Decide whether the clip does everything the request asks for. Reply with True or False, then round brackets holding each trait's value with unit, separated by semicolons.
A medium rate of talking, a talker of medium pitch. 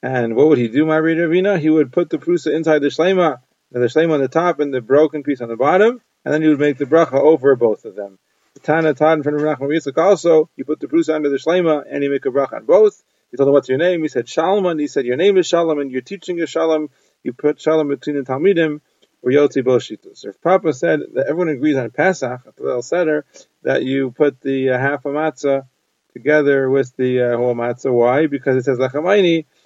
False (235 wpm; 150 Hz)